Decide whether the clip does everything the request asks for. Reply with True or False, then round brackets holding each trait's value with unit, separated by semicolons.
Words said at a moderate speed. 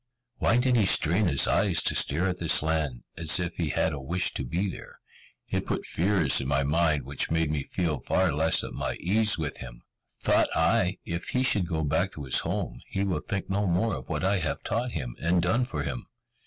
False (225 wpm)